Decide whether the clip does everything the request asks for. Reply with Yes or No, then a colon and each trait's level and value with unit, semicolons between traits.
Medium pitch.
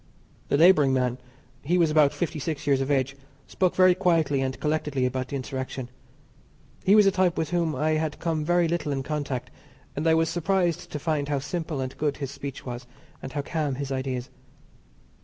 Yes: medium, 150 Hz